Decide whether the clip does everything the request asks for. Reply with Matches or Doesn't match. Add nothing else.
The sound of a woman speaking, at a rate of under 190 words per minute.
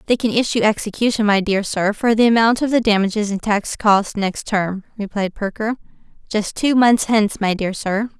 Doesn't match